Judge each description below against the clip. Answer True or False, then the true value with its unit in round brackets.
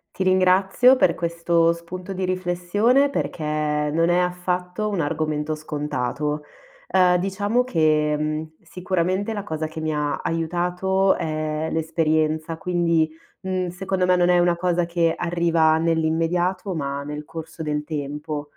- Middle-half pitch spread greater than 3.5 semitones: False (2.7 semitones)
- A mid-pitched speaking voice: True (170 Hz)